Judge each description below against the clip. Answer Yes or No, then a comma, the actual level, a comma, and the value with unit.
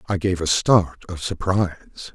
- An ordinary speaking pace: Yes, average, 170 wpm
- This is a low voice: Yes, very low, 90 Hz